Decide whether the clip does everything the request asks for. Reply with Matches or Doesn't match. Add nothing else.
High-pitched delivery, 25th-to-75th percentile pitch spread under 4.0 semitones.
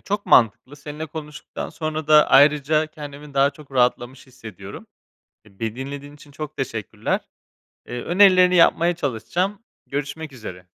Doesn't match